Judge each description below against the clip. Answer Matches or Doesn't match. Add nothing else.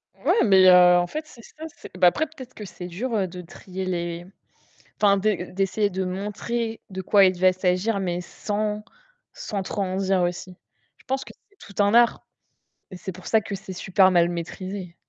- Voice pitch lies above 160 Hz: Matches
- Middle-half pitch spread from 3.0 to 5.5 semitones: Doesn't match